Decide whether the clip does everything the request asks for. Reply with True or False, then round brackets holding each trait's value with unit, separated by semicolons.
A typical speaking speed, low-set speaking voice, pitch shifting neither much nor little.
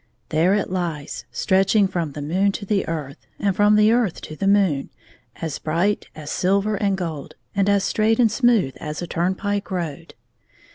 False (180 wpm; 190 Hz; 4.1 semitones)